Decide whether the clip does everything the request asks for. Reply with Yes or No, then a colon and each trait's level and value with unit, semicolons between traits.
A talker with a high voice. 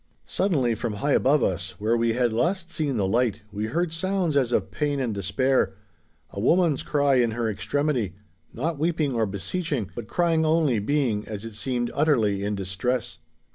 No: low, 120 Hz